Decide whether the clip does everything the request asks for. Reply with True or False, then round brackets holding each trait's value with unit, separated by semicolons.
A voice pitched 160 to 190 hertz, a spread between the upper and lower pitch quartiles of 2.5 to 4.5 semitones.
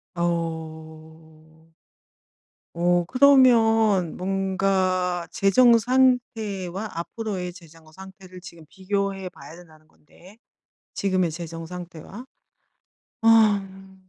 True (185 Hz; 3.3 semitones)